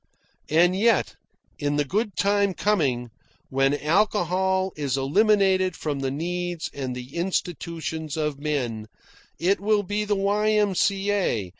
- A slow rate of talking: Yes, slow, 125 wpm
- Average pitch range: No, wide, 5.7 semitones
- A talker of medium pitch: Yes, medium, 175 Hz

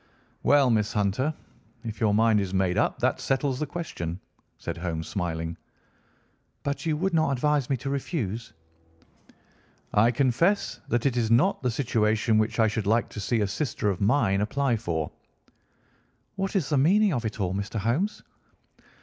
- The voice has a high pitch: No, low, 115 Hz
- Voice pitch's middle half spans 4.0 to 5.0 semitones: No, wide, 5.4 semitones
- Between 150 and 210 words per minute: Yes, average, 165 wpm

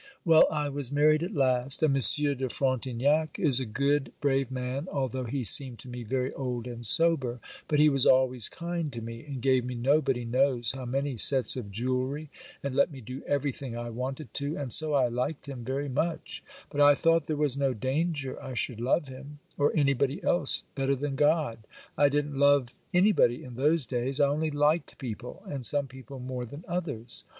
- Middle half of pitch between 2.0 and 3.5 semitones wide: Yes, narrow, 2.6 semitones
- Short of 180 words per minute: No, average, 195 wpm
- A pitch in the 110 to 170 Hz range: Yes, low, 135 Hz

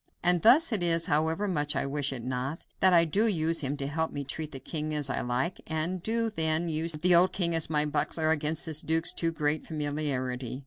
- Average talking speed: No, fast, 230 wpm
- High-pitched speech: No, medium, 160 Hz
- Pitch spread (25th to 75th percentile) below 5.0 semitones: Yes, narrow, 2.6 semitones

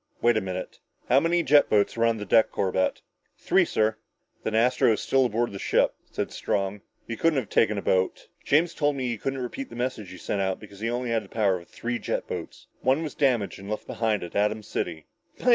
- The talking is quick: Yes, fast, 230 wpm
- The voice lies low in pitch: Yes, low, 110 Hz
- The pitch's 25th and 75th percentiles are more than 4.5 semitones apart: No, average, 4.1 semitones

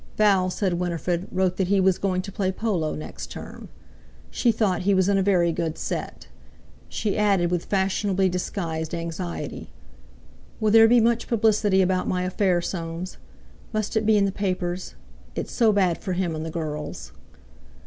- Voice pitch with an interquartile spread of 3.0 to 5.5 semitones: No, narrow, 2.6 semitones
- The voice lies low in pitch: No, medium, 185 Hz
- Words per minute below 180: Yes, average, 170 wpm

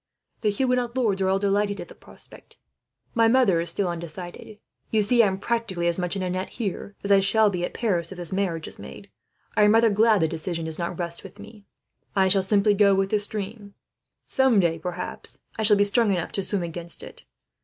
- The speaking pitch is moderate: No, high, 200 Hz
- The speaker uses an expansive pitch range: No, average, 3.2 semitones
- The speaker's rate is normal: No, fast, 225 wpm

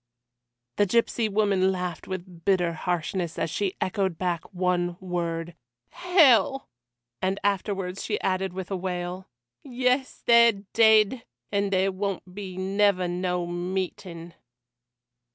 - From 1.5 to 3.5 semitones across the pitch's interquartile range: Yes, narrow, 2.4 semitones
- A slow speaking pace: Yes, slow, 125 wpm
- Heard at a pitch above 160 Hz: Yes, high, 190 Hz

